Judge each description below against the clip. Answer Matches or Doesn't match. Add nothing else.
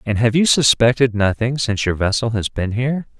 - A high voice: Doesn't match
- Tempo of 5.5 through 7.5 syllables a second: Matches